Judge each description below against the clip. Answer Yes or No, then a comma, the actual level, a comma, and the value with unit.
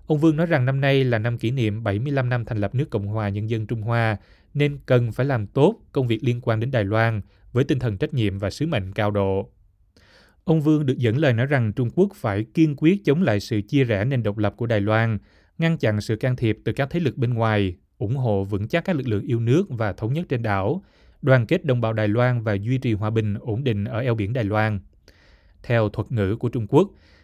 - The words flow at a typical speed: No, fast, 255 wpm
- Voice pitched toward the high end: No, low, 115 Hz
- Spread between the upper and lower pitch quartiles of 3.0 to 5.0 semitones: Yes, average, 4.3 semitones